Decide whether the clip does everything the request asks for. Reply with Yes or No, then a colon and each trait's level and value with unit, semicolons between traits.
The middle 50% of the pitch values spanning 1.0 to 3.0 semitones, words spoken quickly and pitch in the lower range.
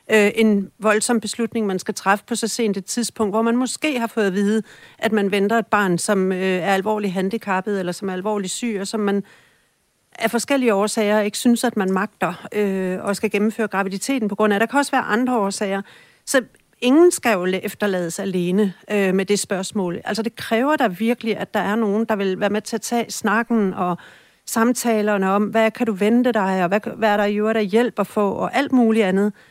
No: narrow, 2.5 semitones; fast, 220 wpm; high, 210 Hz